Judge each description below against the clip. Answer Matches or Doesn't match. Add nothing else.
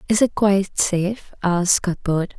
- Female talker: Matches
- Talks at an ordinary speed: Matches